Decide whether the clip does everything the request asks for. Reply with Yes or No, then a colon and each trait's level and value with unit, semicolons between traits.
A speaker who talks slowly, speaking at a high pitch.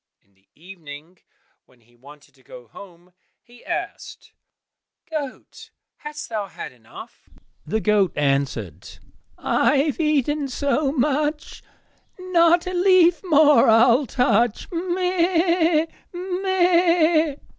Yes: slow, 105 wpm; very high, 285 Hz